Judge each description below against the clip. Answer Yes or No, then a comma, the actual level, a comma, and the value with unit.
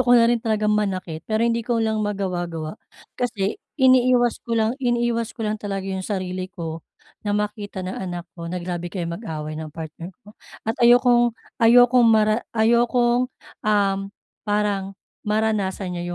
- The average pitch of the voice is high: Yes, high, 210 Hz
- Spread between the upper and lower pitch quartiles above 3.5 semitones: Yes, average, 4.0 semitones